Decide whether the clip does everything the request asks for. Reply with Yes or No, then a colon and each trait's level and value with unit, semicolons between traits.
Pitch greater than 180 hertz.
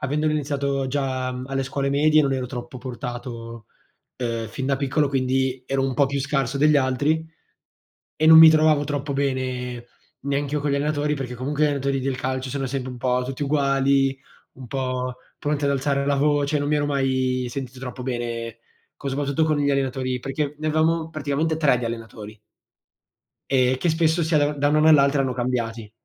No: low, 135 Hz